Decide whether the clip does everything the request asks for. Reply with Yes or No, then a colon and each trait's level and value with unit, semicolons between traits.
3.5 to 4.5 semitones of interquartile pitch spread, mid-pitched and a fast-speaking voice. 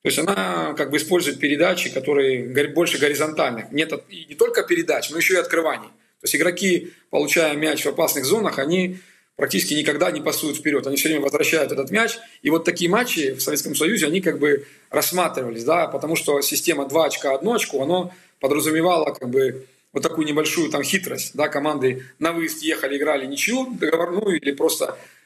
Yes: average, 3.9 semitones; medium, 160 Hz; fast, 185 wpm